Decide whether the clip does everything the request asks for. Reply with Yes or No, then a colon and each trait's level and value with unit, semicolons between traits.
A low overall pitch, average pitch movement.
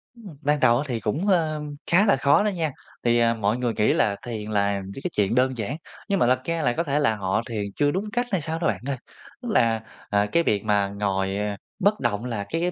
No: low, 125 Hz; wide, 7.5 semitones